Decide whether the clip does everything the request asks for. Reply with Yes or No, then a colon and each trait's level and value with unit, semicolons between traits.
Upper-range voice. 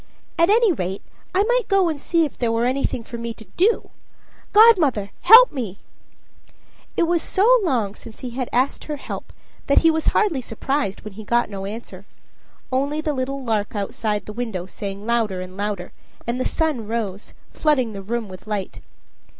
Yes: high, 240 Hz